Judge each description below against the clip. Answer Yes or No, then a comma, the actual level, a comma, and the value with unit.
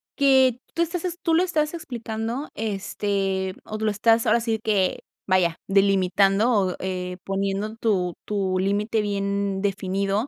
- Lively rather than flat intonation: No, average, 2.9 semitones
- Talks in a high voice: Yes, high, 205 Hz